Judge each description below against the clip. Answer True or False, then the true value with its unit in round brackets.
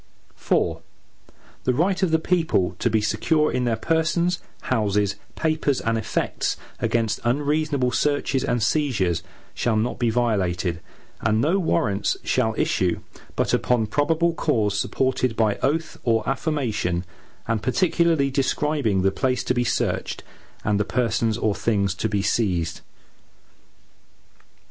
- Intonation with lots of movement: True (5.9 semitones)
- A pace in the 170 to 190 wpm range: False (135 wpm)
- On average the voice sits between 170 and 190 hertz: False (120 Hz)